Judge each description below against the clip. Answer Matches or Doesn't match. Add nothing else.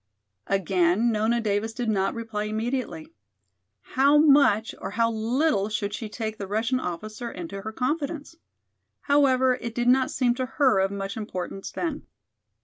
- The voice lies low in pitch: Doesn't match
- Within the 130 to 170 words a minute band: Matches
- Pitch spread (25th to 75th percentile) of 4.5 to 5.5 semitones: Doesn't match